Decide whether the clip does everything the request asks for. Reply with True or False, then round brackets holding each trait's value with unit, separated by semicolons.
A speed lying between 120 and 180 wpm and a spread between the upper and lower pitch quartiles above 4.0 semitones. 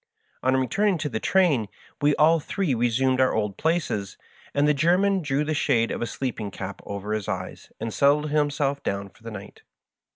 False (190 wpm; 5.6 semitones)